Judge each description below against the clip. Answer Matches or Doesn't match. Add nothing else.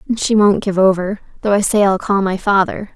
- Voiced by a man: Doesn't match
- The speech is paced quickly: Matches